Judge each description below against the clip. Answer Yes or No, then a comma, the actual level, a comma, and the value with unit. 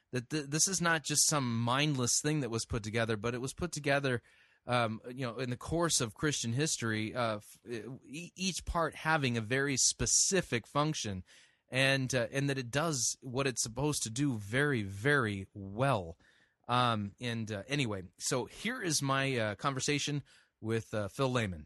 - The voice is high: No, low, 130 Hz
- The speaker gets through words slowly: No, average, 170 wpm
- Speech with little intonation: No, average, 4.2 semitones